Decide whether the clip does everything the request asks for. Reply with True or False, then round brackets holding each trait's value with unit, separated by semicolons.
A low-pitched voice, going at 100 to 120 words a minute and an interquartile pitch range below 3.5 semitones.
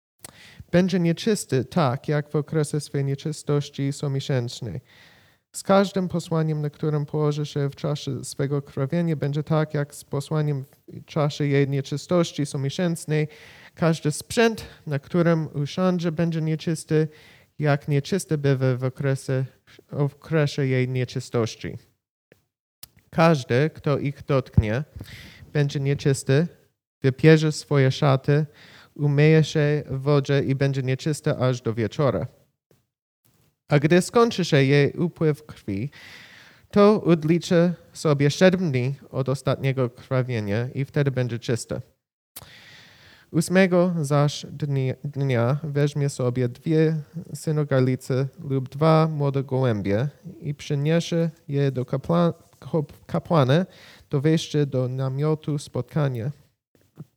False (145 Hz; 110 wpm; 2.8 semitones)